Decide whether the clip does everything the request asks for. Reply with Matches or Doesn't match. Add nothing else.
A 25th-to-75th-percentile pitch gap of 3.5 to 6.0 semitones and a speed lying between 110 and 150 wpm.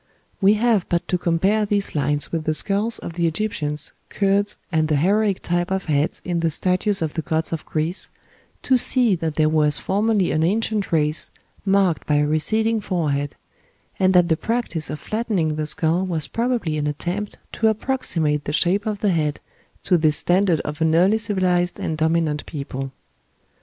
Doesn't match